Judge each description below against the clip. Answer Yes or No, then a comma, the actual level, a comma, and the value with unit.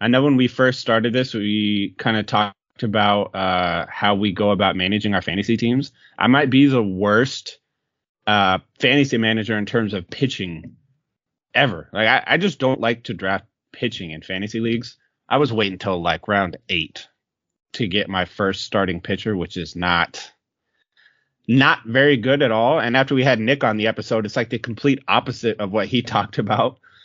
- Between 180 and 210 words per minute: Yes, average, 190 wpm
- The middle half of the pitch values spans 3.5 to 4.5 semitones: Yes, average, 4.0 semitones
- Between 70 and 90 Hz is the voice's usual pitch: No, low, 110 Hz